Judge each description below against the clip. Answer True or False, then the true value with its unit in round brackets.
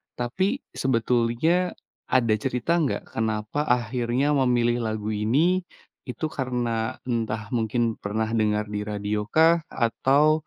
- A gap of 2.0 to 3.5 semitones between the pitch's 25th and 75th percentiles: False (4.0 semitones)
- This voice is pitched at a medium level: False (120 Hz)